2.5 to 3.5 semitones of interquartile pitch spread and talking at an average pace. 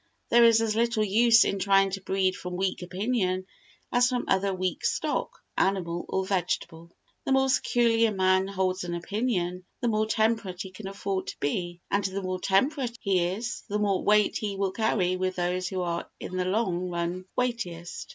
Yes: average, 3.1 semitones; average, 190 wpm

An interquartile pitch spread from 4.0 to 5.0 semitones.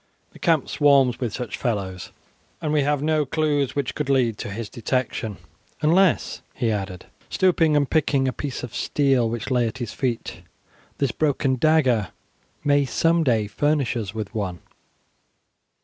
Yes: average, 4.5 semitones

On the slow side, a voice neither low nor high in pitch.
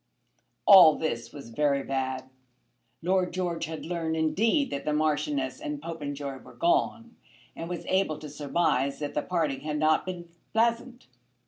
No: average, 150 wpm; medium, 155 Hz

